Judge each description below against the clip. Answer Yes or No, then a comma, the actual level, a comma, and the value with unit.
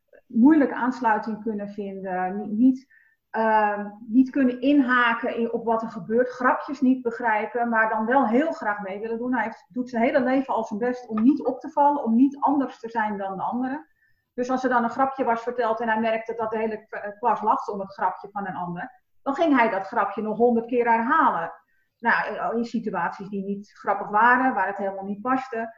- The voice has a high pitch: Yes, high, 230 Hz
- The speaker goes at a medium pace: No, fast, 210 wpm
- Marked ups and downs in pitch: No, average, 3.2 semitones